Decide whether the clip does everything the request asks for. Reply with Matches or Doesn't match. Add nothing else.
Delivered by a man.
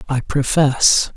Matches